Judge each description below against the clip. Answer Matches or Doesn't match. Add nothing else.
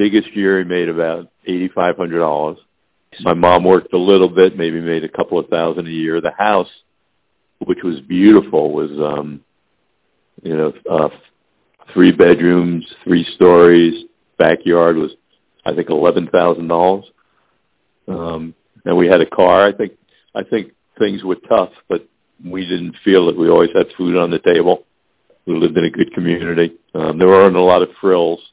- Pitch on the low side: Matches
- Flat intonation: Matches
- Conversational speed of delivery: Matches